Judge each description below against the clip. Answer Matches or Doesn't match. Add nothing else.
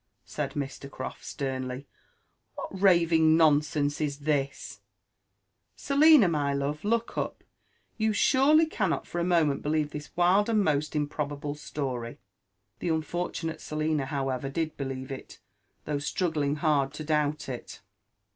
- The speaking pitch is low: Doesn't match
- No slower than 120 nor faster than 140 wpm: Matches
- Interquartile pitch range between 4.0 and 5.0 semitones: Doesn't match